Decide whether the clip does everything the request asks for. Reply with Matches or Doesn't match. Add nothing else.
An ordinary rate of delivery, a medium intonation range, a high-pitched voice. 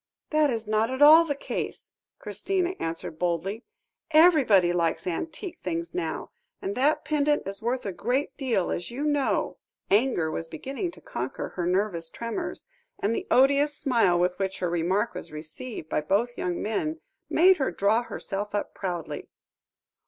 Doesn't match